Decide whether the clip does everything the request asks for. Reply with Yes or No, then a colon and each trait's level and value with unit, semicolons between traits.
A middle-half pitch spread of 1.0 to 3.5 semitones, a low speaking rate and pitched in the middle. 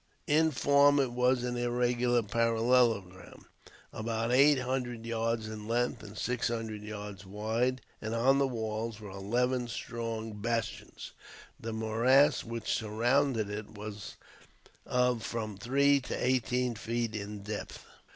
No: narrow, 2.4 semitones; slow, 130 wpm; low, 115 Hz